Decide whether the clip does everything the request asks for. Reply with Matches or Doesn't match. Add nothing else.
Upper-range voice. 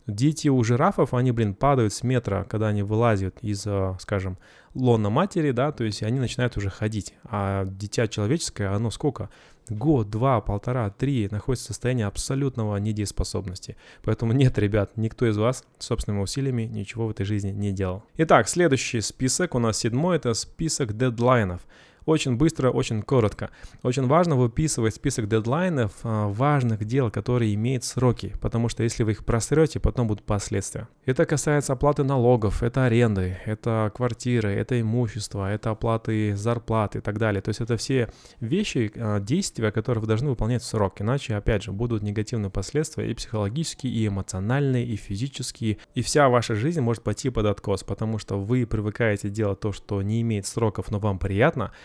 Doesn't match